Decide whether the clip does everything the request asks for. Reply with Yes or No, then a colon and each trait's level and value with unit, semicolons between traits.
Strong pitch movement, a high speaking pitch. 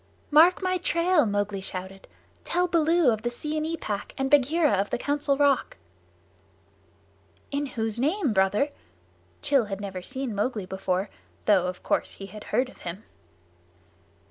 Yes: wide, 7.0 semitones; high, 245 Hz